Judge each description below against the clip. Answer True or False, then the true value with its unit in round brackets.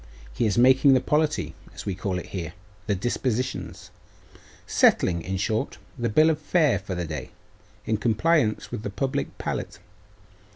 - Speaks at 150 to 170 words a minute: True (160 wpm)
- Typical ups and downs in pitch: False (6.1 semitones)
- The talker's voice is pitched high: False (110 Hz)